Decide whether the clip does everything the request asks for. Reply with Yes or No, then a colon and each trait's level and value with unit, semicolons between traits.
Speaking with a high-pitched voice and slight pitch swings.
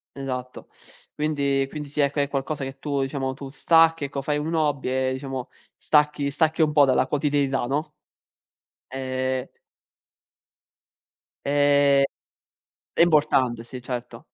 No: medium, 140 Hz; narrow, 2.0 semitones